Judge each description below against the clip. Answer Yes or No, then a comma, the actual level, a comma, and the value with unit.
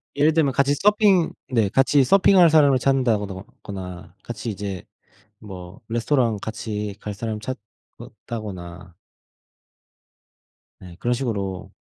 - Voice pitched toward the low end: Yes, low, 110 Hz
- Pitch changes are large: Yes, wide, 5.7 semitones